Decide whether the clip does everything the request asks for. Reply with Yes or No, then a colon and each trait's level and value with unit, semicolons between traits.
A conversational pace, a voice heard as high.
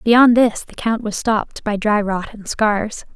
No: fast, 210 wpm; high, 215 Hz